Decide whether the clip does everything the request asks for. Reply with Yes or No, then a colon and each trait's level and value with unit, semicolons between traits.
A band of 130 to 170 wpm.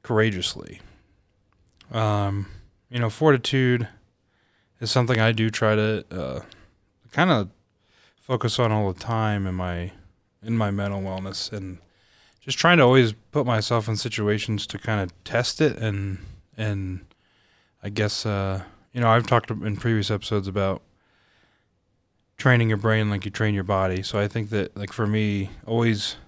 Yes: average, 155 wpm